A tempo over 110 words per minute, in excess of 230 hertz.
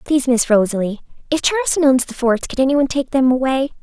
Yes: fast, 205 wpm; very high, 255 Hz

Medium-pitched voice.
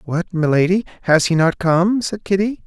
Yes: medium, 180 Hz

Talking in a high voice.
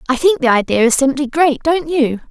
Yes: very high, 280 Hz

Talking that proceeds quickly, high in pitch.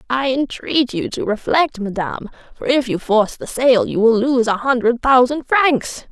No: average, 185 wpm; high, 245 Hz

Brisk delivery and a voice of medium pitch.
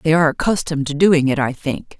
Yes: fast, 240 wpm; medium, 150 Hz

